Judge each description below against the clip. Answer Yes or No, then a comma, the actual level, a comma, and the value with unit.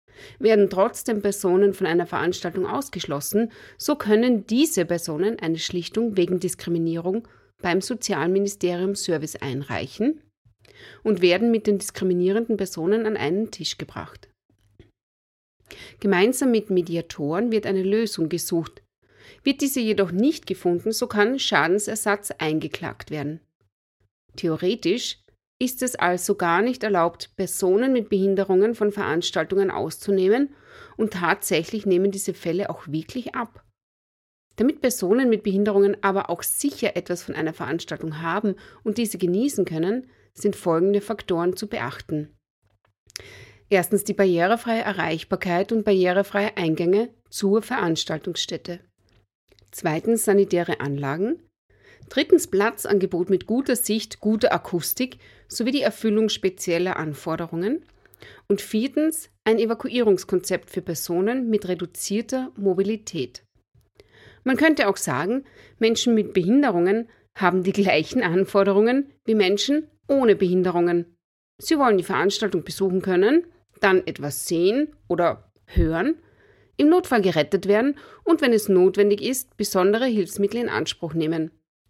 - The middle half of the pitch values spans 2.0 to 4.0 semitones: No, average, 4.5 semitones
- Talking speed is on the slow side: Yes, slow, 120 wpm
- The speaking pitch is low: No, high, 195 Hz